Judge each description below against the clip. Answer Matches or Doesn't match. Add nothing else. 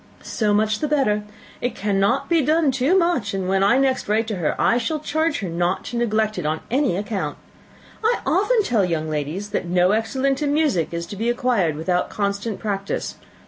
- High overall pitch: Matches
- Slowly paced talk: Doesn't match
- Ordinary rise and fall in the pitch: Doesn't match